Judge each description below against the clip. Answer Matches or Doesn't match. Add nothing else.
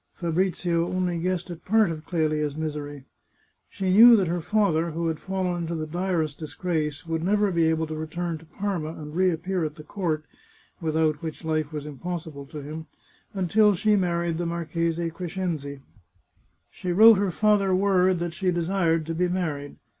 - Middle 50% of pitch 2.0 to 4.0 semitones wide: Matches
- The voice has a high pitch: Doesn't match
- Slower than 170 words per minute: Doesn't match